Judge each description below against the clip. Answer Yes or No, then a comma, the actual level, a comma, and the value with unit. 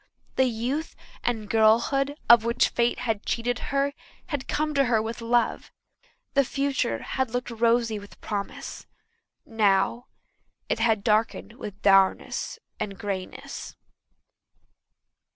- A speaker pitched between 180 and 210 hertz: No, high, 230 Hz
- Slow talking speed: Yes, slow, 120 wpm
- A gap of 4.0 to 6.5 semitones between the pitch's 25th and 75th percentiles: No, average, 2.9 semitones